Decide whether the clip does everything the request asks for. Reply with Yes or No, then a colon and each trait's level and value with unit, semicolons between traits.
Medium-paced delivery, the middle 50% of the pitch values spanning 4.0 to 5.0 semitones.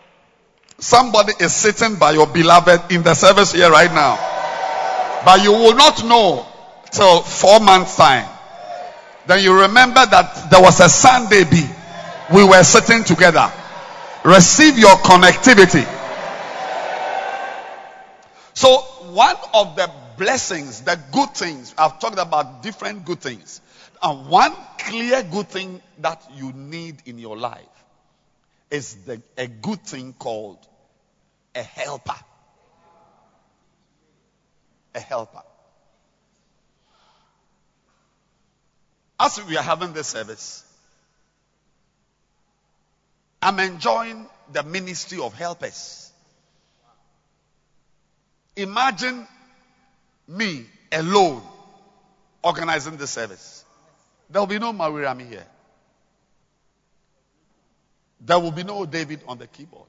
No: slow, 105 wpm; average, 4.6 semitones